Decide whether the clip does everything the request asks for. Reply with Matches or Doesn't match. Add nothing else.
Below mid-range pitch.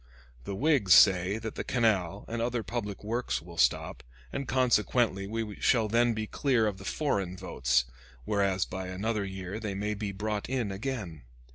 Matches